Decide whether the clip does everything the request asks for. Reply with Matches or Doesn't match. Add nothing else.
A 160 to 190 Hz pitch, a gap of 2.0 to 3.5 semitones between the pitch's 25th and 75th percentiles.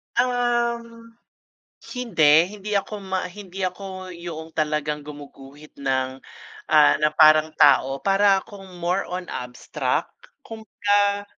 Doesn't match